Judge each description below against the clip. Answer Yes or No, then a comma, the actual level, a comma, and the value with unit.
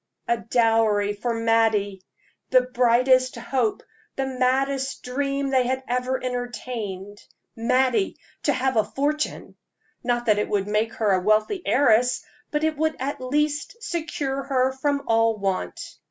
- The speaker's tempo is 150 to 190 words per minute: No, average, 140 wpm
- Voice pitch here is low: No, very high, 250 Hz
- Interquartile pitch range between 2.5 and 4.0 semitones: Yes, average, 3.3 semitones